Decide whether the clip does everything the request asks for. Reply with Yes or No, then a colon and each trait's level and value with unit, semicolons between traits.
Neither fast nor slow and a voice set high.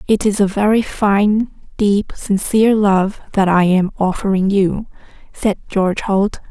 Yes: average, 150 wpm; high, 200 Hz